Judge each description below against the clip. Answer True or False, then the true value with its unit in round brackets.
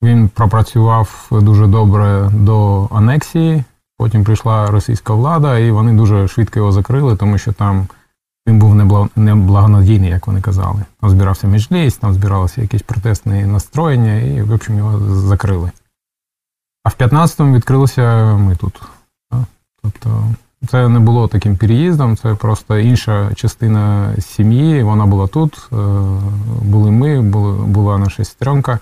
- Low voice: True (105 Hz)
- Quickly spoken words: False (130 wpm)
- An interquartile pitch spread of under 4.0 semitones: True (2.4 semitones)